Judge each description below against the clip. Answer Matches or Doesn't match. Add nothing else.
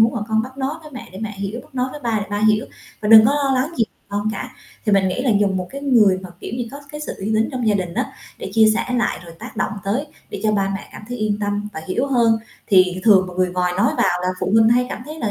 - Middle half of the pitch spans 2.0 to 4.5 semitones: Matches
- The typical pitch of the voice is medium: Doesn't match